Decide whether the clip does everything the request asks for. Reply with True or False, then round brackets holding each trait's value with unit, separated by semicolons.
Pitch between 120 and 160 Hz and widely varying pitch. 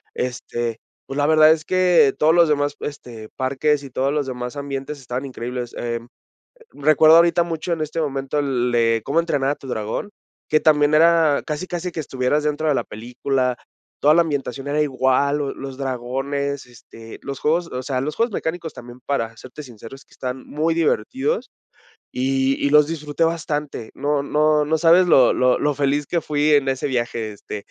False (140 Hz; 3.2 semitones)